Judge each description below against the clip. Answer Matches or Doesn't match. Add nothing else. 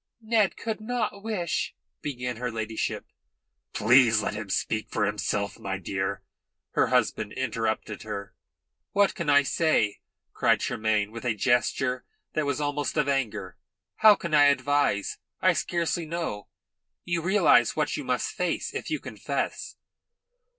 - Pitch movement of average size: Doesn't match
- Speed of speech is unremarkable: Matches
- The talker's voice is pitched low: Matches